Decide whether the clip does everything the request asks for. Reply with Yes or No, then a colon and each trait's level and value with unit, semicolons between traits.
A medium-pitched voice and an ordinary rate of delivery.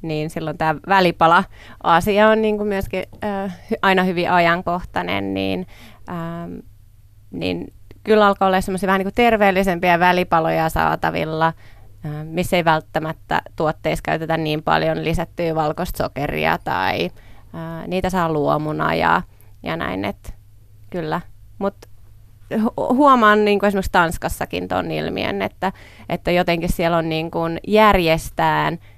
Yes: medium, 165 Hz; average, 120 wpm